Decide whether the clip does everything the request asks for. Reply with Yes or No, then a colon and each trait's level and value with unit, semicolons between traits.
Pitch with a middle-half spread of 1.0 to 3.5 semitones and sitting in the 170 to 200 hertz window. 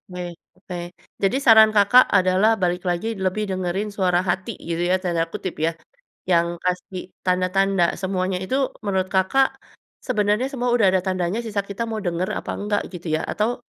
Yes: average, 2.9 semitones; high, 190 Hz